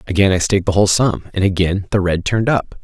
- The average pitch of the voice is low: Yes, very low, 95 Hz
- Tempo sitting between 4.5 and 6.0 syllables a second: No, 6.7 syllables/s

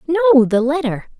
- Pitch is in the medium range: No, very high, 255 Hz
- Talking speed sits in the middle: Yes, average, 150 wpm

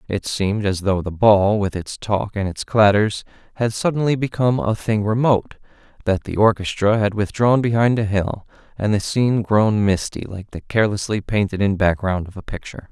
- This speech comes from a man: Yes, male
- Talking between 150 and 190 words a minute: Yes, average, 180 wpm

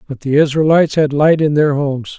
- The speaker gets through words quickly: Yes, fast, 220 wpm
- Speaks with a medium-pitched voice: Yes, medium, 145 Hz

